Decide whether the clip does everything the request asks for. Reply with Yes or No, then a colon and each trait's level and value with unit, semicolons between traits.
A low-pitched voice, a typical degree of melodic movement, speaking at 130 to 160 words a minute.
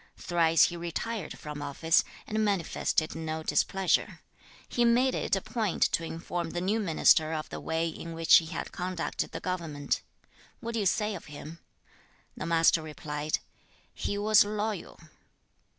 No: medium, 170 Hz; average, 4.2 semitones; average, 155 wpm